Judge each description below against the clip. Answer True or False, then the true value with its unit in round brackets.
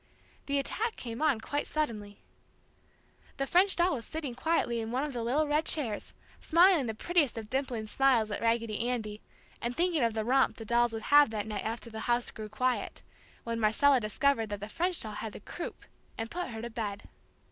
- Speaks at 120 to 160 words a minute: False (200 wpm)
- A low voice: False (240 Hz)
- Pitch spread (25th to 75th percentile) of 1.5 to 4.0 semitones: False (4.8 semitones)